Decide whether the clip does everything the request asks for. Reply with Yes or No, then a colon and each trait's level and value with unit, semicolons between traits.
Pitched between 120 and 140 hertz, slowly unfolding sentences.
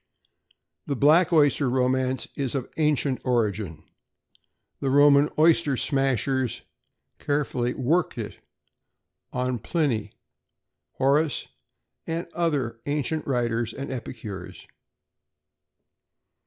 Yes: low, 135 Hz; slow, 85 wpm